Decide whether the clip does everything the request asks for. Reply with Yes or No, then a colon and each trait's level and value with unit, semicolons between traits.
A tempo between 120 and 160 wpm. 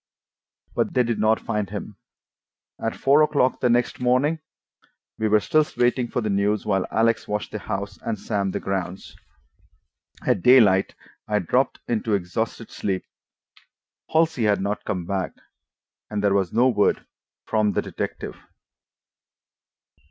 Yes: average, 140 wpm